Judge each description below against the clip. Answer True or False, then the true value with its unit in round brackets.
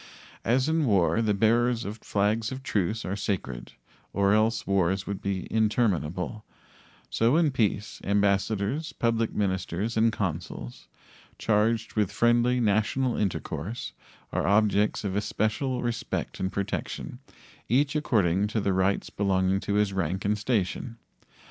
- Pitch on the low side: True (105 Hz)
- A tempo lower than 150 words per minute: True (135 wpm)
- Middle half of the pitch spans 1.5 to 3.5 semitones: True (2.9 semitones)